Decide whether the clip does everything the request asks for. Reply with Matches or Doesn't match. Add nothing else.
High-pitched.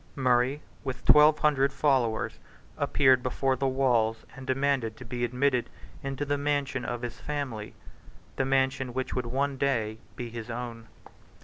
Doesn't match